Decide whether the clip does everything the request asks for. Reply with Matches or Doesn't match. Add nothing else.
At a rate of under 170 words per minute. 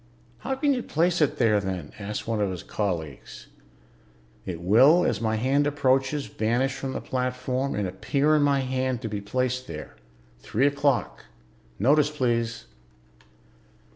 Matches